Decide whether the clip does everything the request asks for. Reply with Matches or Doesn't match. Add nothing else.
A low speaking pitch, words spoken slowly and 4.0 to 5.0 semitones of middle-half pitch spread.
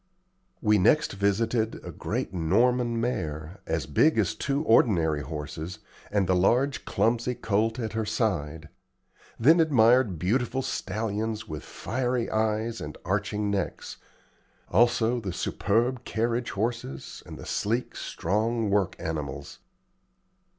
Matches